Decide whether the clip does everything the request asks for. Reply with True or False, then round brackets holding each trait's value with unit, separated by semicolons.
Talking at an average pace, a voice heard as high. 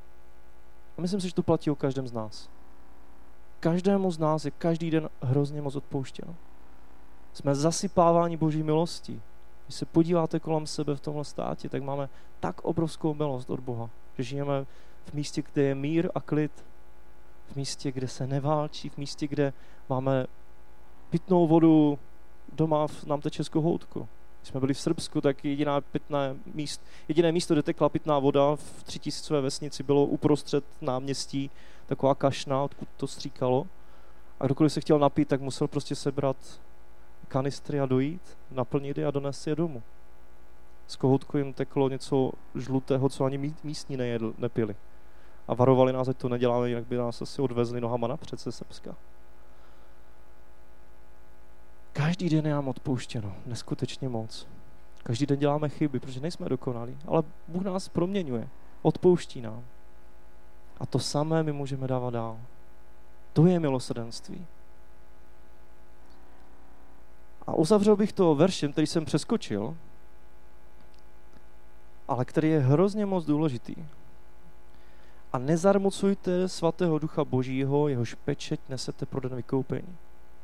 False (140 wpm; 135 Hz)